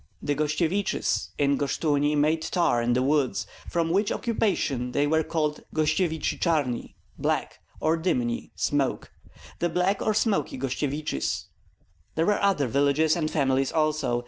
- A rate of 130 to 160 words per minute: Yes, average, 140 wpm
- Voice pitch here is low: No, medium, 150 Hz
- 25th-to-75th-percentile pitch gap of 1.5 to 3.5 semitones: Yes, average, 3.1 semitones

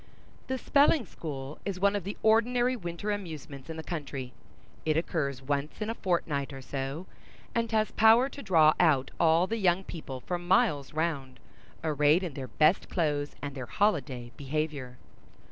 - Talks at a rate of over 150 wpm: Yes, average, 165 wpm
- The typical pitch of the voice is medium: Yes, medium, 160 Hz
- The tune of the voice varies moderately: No, wide, 6.2 semitones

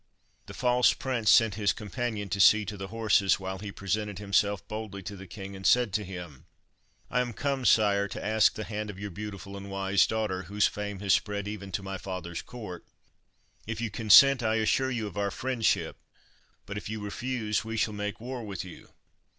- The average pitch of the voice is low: Yes, low, 105 Hz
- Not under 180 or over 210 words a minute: Yes, average, 200 wpm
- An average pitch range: No, narrow, 2.2 semitones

